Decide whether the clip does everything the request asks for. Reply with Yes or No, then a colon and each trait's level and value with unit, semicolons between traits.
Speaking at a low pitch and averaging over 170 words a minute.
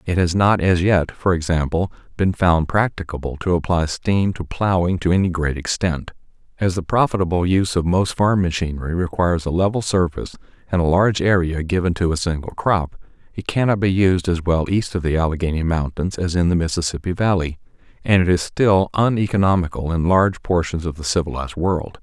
Yes: very low, 90 Hz; average, 185 wpm